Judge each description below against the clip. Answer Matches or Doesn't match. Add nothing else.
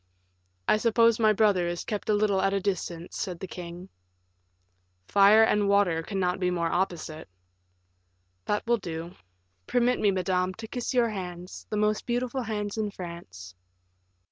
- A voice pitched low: Doesn't match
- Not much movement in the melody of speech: Doesn't match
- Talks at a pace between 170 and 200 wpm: Doesn't match